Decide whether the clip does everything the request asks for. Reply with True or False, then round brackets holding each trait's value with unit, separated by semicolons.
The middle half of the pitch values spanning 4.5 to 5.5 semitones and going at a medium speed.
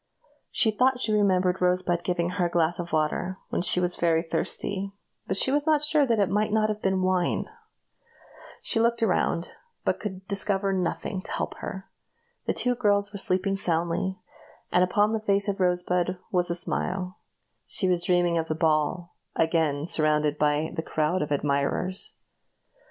False (3.0 semitones; 175 wpm)